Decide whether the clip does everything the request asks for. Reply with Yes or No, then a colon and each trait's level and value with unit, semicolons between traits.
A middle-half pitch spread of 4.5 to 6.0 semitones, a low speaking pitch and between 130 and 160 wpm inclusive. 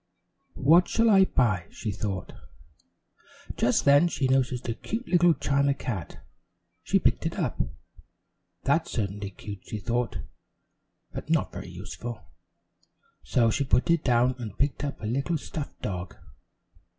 Yes: average, 5.1 semitones; low, 125 Hz; average, 140 wpm